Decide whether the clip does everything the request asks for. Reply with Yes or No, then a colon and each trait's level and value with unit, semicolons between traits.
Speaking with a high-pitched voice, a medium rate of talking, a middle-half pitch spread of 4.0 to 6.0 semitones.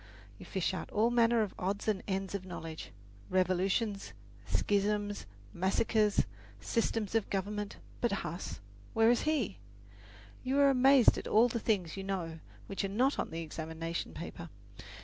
No: high, 200 Hz; average, 150 wpm; average, 3.6 semitones